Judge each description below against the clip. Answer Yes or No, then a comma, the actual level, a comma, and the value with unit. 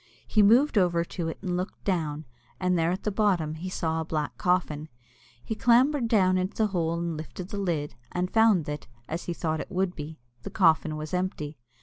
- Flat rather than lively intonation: No, average, 3.4 semitones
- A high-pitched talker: No, medium, 180 Hz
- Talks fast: Yes, fast, 210 wpm